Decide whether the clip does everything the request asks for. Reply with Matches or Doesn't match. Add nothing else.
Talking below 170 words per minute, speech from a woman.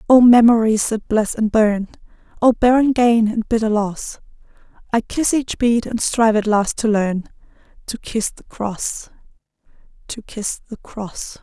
Matches